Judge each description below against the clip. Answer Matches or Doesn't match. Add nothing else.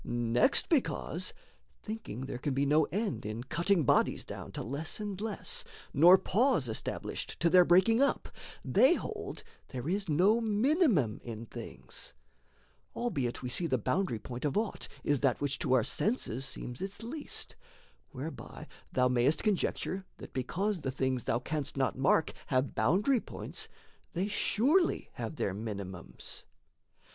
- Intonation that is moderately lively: Doesn't match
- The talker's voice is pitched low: Doesn't match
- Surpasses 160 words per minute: Doesn't match